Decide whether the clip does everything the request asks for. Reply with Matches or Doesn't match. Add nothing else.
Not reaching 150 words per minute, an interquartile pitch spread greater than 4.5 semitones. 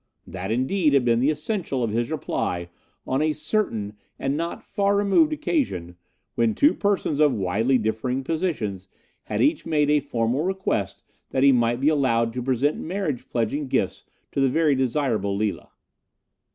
Doesn't match